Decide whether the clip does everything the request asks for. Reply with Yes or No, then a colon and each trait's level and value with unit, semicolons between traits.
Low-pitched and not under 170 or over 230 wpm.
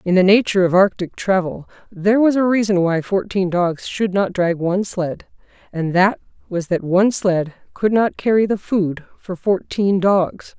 No: high, 190 Hz; average, 180 wpm